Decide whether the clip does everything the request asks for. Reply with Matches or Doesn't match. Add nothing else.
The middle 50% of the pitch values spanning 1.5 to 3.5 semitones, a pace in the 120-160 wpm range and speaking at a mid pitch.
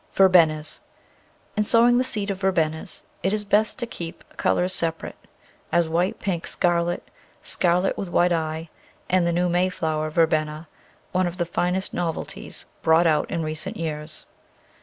Matches